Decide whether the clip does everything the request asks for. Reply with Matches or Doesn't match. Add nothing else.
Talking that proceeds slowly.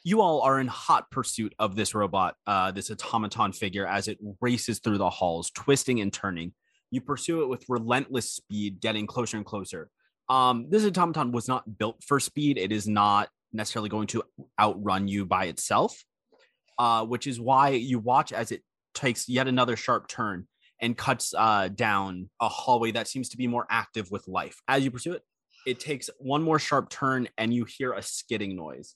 Doesn't match